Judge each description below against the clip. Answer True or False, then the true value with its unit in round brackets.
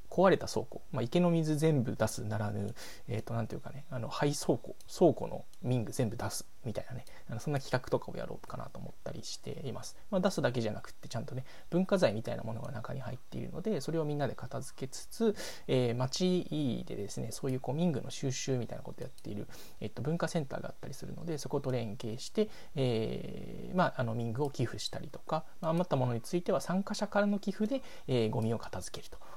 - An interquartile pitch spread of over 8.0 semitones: False (5.6 semitones)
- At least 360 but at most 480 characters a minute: True (430 characters per minute)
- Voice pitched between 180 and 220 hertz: False (135 Hz)